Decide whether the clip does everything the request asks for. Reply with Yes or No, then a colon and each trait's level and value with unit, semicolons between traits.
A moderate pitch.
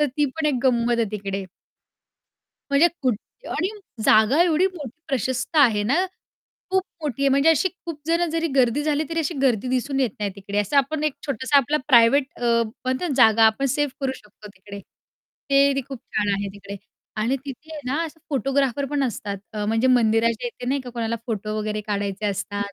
No: very high, 255 Hz